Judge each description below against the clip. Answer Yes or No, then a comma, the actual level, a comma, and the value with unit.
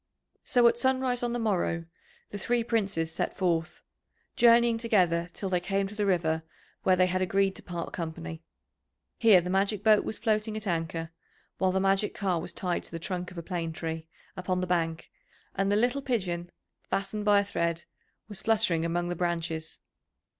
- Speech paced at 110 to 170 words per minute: No, average, 185 wpm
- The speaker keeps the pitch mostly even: No, average, 3.8 semitones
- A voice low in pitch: No, medium, 185 Hz